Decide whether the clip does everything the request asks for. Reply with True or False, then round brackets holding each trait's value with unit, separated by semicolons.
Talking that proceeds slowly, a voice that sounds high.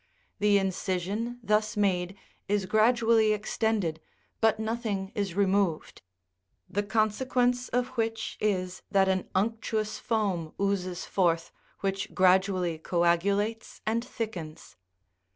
True (110 wpm; 205 Hz)